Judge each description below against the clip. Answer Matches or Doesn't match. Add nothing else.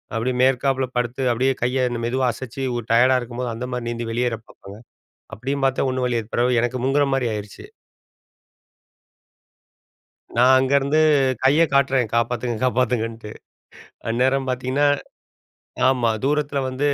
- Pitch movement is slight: Matches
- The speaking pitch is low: Matches